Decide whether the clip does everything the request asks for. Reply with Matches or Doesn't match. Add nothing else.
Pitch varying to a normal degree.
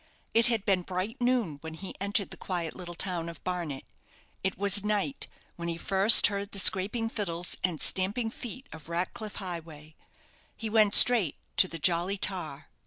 Matches